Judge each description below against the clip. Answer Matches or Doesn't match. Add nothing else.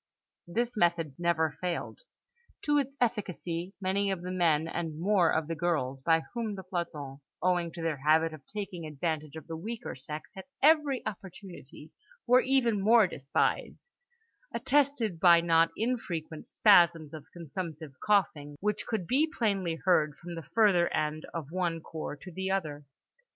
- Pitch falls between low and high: Matches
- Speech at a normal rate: Matches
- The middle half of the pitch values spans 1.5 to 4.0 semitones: Doesn't match